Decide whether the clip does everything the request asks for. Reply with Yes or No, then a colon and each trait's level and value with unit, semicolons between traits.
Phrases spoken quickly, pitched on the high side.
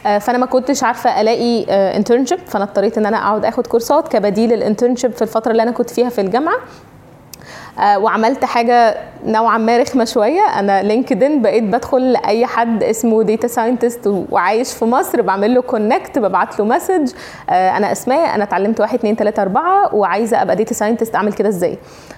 Yes: fast, 170 wpm; high, 230 Hz